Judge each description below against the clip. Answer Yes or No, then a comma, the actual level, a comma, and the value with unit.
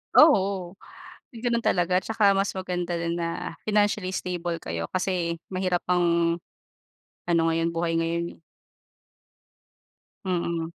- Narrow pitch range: Yes, narrow, 2.1 semitones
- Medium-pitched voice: Yes, medium, 175 Hz